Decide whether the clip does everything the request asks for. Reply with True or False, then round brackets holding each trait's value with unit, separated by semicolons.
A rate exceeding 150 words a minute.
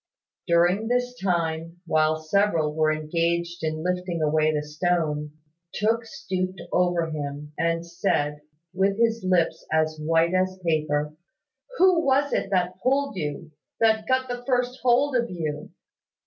False (140 wpm)